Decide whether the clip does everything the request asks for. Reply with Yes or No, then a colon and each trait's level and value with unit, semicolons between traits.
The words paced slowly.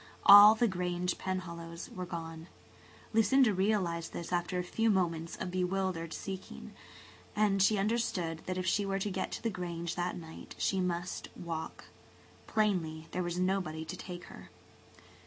No: average, 155 wpm